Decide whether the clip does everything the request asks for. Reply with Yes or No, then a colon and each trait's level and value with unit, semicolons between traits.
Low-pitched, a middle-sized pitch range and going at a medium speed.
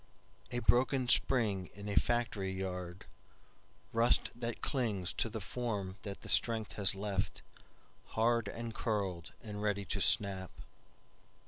No: low, 105 Hz; average, 3.4 semitones; slow, 120 wpm